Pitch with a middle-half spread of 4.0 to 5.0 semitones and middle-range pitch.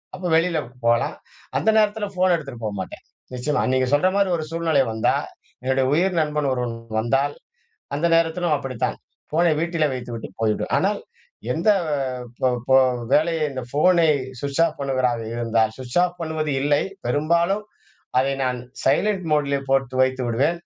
Yes: average, 4.6 semitones; medium, 145 Hz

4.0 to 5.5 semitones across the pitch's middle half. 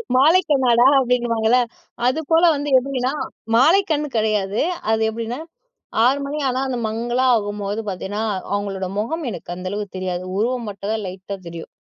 Yes: average, 4.3 semitones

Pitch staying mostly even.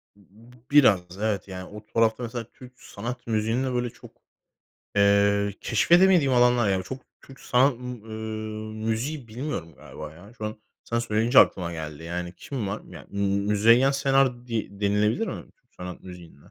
No: average, 3.6 semitones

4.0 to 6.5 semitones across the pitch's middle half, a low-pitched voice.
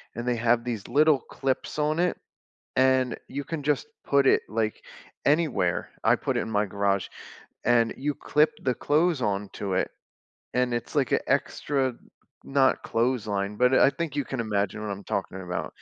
Yes: average, 5.1 semitones; low, 125 Hz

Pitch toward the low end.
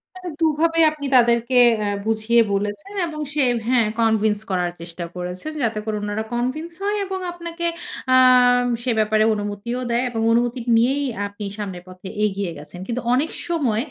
No: high, 235 Hz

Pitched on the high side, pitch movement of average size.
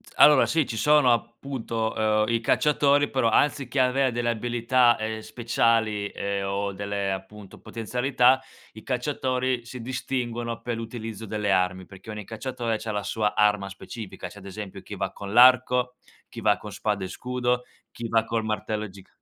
No: low, 115 Hz; average, 3.3 semitones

